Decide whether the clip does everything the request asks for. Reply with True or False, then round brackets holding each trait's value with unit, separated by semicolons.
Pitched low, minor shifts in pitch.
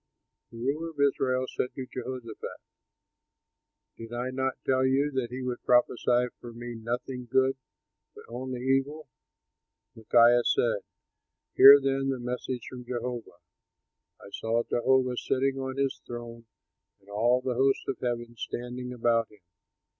True (125 Hz; 1.9 semitones)